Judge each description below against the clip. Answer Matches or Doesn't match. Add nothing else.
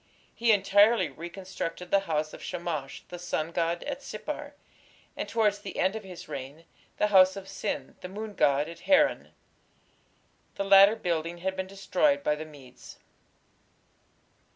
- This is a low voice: Doesn't match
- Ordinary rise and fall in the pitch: Matches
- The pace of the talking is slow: Doesn't match